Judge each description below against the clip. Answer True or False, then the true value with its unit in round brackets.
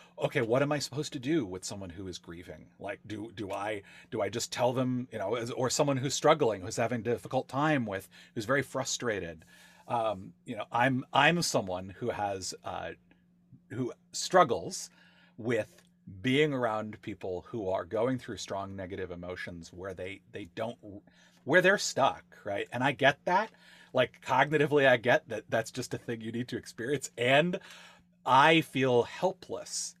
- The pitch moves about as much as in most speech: False (5.9 semitones)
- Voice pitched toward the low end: True (120 Hz)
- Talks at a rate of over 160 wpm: True (175 wpm)